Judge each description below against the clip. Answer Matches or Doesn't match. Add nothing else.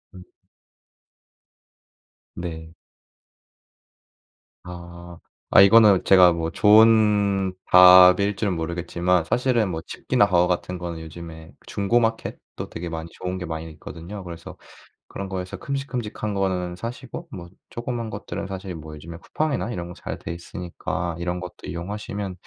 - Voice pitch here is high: Doesn't match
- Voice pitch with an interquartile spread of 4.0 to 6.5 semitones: Doesn't match